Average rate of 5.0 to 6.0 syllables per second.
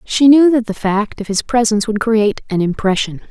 Yes: 5.6 syllables/s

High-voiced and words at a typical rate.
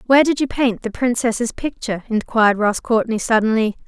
Yes: high, 230 Hz; average, 170 wpm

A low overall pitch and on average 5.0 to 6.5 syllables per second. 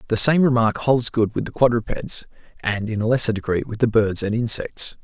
Yes: low, 115 Hz; 5.4 syllables/s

